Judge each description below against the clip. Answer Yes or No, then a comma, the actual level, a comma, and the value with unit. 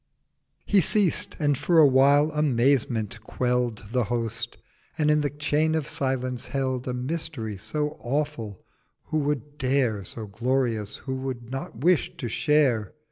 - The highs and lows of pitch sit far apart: No, average, 4.0 semitones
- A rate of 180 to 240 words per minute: No, slow, 135 wpm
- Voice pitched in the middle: No, low, 130 Hz